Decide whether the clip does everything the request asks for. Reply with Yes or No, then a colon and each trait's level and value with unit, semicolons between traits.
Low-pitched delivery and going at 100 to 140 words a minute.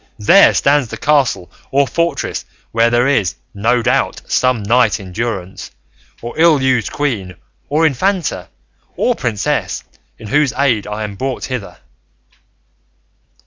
Yes: low, 125 Hz; slow, 135 wpm